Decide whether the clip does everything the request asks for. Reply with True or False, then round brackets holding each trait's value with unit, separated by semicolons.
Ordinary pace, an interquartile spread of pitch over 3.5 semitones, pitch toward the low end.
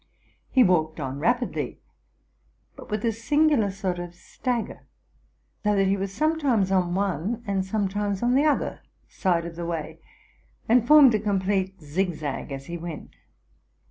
False (155 wpm; 4.8 semitones; 195 Hz)